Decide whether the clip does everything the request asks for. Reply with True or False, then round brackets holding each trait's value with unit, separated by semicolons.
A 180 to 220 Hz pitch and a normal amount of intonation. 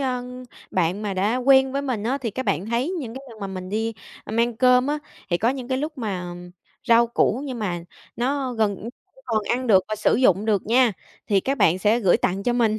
False (230 Hz; 4.1 semitones)